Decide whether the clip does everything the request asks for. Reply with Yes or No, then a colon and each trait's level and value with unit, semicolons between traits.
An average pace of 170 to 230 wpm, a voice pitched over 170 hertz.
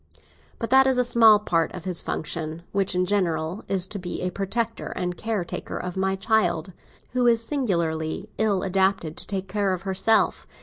Yes: average, 180 wpm; high, 190 Hz